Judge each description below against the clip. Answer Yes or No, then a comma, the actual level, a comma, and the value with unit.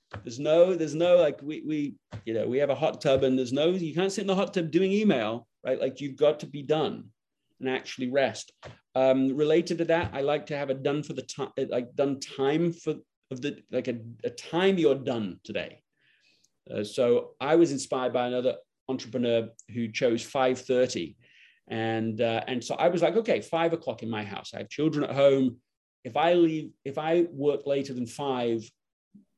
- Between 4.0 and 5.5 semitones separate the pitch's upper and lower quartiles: Yes, average, 4.6 semitones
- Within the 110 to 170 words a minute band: No, fast, 205 wpm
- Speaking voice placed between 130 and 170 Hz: Yes, medium, 140 Hz